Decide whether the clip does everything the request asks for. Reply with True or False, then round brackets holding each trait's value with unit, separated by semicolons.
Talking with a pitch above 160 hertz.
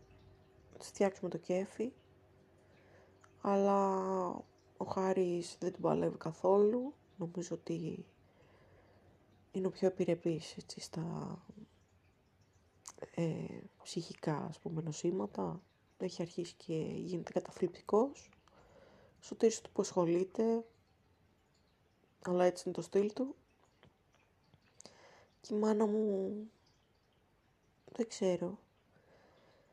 True (185 Hz)